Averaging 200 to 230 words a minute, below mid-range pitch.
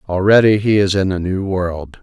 Yes: fast, 205 wpm; very low, 95 Hz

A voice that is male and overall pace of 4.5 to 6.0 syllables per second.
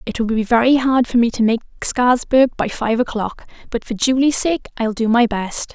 No: female; 5.0 syllables/s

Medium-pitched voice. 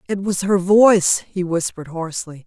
Yes: medium, 180 Hz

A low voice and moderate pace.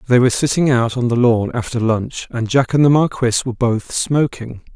No: low, 125 Hz; fast, 215 wpm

